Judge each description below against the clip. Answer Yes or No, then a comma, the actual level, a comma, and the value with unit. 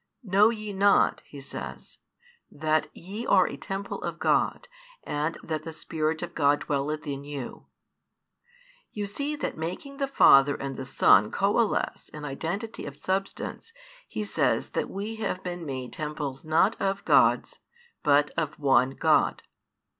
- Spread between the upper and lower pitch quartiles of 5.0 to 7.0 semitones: Yes, wide, 5.6 semitones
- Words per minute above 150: No, average, 145 wpm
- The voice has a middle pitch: Yes, medium, 160 Hz